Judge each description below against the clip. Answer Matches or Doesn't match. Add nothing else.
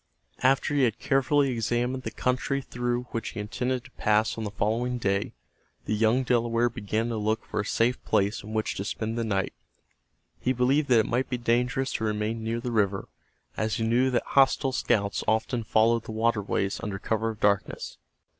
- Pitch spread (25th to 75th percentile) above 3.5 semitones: Doesn't match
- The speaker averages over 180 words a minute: Matches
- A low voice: Matches